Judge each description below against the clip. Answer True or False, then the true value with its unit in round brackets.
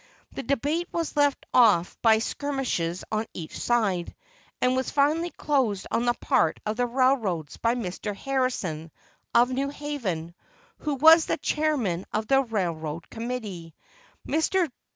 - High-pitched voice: True (240 Hz)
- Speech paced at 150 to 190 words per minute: False (135 wpm)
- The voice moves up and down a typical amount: False (6.8 semitones)